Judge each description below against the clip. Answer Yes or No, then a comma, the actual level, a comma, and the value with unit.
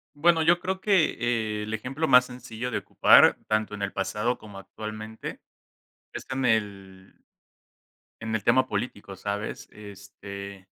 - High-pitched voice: No, low, 110 Hz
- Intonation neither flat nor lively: Yes, average, 3.7 semitones